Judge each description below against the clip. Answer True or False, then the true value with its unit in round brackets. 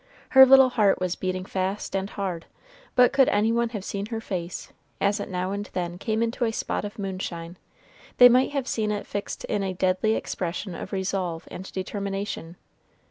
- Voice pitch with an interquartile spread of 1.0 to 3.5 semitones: True (3.2 semitones)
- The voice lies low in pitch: False (200 Hz)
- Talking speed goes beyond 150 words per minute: True (190 wpm)